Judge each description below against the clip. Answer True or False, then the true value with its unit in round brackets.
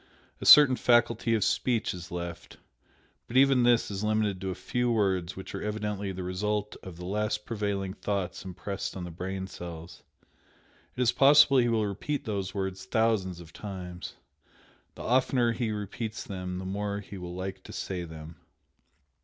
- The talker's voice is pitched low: True (100 Hz)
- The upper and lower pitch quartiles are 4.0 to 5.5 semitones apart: False (3.4 semitones)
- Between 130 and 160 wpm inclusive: False (170 wpm)